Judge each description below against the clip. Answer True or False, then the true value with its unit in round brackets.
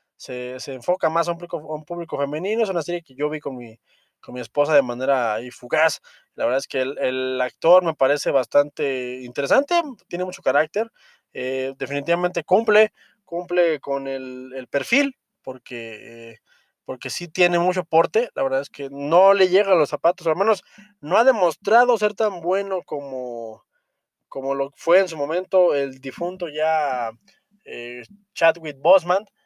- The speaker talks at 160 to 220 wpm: True (175 wpm)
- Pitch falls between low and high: True (160 Hz)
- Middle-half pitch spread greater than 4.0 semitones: True (5.6 semitones)